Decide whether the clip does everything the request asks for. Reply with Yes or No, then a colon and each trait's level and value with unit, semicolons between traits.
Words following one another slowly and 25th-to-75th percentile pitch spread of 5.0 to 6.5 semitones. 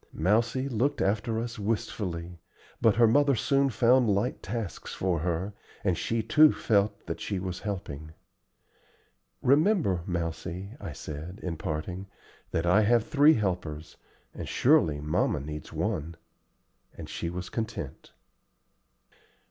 Yes: slow, 130 wpm; wide, 5.5 semitones